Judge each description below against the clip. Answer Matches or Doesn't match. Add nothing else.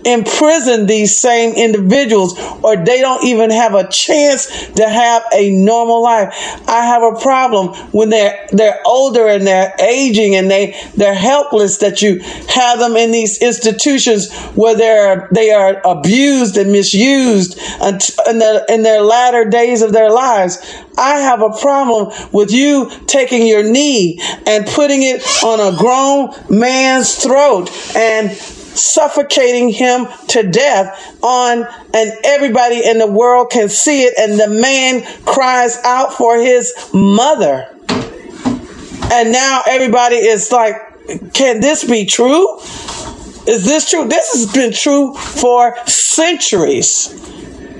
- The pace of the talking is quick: Doesn't match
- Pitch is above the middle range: Matches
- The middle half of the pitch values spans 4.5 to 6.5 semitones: Doesn't match